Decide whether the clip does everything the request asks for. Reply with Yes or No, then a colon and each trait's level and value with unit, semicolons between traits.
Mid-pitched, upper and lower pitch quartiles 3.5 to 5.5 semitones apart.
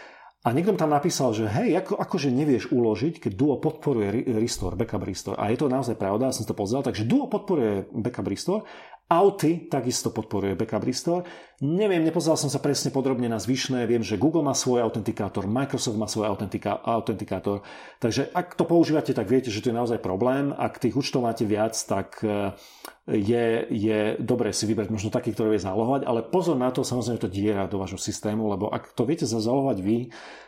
No: low, 120 Hz; average, 4.5 semitones